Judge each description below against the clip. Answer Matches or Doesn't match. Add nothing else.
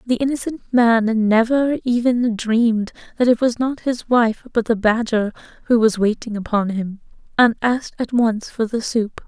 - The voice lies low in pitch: Doesn't match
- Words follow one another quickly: Doesn't match